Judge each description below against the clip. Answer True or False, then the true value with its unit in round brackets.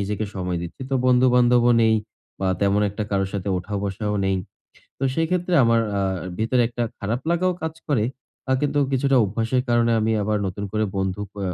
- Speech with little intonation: False (4.1 semitones)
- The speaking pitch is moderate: False (110 Hz)